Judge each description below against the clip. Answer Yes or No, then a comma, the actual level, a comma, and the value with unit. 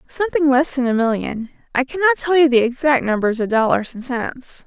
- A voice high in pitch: Yes, very high, 265 Hz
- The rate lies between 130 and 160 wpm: No, fast, 205 wpm